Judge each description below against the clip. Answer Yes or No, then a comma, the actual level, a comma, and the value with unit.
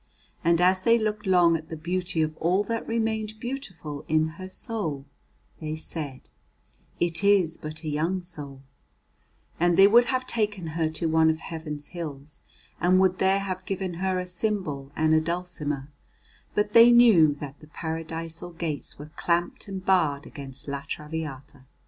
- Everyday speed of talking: Yes, average, 165 wpm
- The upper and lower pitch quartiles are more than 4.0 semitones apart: No, average, 3.6 semitones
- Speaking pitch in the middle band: Yes, medium, 170 Hz